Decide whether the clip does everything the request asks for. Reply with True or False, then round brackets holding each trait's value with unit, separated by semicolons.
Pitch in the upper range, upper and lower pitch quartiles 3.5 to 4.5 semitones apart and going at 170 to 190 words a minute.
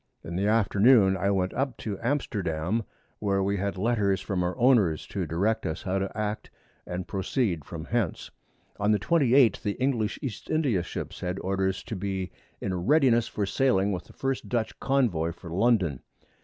False (100 Hz; 4.1 semitones; 180 wpm)